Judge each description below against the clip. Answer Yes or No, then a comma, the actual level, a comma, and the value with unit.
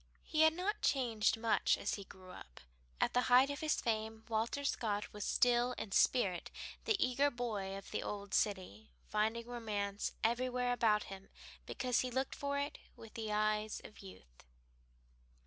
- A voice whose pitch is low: No, high, 225 Hz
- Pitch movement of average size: Yes, average, 3.3 semitones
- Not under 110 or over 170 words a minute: Yes, average, 165 wpm